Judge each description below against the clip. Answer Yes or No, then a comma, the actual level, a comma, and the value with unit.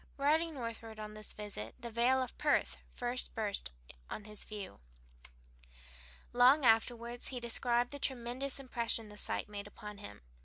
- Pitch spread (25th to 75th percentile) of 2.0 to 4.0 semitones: Yes, average, 3.0 semitones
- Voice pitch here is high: Yes, high, 235 Hz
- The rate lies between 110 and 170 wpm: Yes, average, 150 wpm